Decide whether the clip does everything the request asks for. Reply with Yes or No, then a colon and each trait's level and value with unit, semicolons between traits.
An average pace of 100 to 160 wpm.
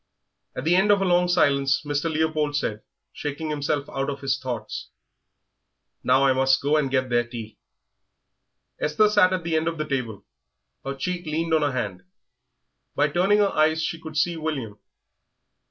No: average, 175 wpm